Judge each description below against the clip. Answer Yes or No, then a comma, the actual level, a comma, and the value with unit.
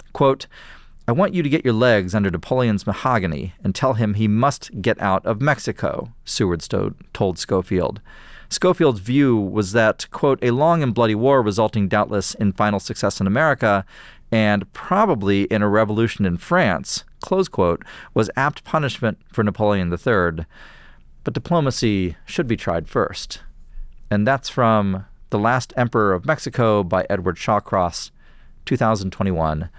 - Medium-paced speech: Yes, average, 150 wpm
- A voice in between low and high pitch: No, low, 110 Hz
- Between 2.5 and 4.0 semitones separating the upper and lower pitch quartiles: No, average, 4.4 semitones